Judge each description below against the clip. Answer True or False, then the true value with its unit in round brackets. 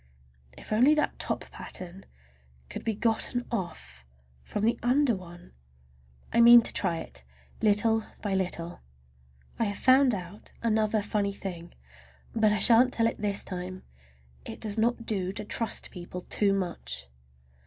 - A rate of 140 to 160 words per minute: True (150 wpm)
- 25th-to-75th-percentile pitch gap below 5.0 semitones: True (3.9 semitones)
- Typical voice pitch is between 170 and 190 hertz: False (210 Hz)